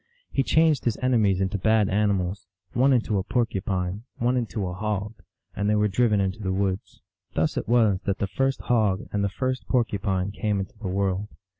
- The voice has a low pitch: Yes, low, 105 Hz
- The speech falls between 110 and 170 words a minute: No, average, 190 wpm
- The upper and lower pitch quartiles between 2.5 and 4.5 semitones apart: Yes, average, 3.3 semitones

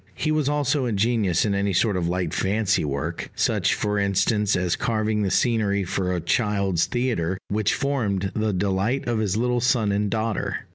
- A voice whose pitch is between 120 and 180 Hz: No, low, 105 Hz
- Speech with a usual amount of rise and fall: Yes, average, 3.3 semitones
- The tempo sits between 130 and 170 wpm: No, average, 180 wpm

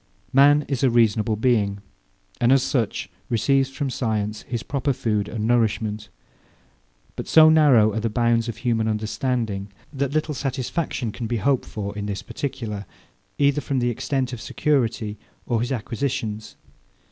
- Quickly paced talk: No, average, 155 wpm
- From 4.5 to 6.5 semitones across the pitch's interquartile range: No, average, 3.9 semitones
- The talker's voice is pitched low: Yes, low, 120 Hz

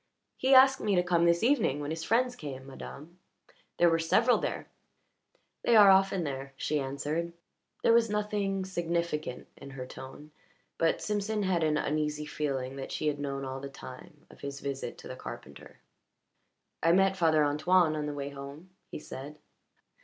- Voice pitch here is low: No, medium, 160 Hz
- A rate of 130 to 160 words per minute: No, average, 175 wpm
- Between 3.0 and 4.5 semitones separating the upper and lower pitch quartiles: No, average, 5.3 semitones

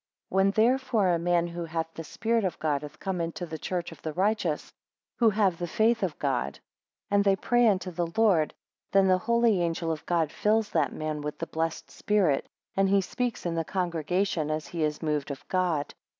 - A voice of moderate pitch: Yes, medium, 175 Hz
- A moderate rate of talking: No, fast, 210 wpm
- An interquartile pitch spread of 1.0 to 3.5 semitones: No, average, 3.9 semitones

